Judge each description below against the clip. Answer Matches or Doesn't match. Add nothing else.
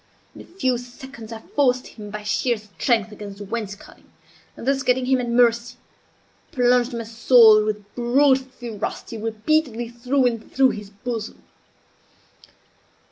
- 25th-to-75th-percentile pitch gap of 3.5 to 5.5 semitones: Doesn't match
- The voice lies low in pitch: Doesn't match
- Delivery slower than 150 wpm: Matches